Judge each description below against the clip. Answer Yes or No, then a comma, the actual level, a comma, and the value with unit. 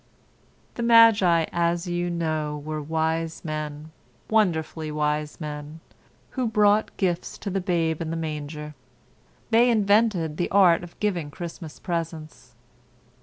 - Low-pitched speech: No, medium, 165 Hz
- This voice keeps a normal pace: No, slow, 120 wpm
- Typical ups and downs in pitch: Yes, average, 3.6 semitones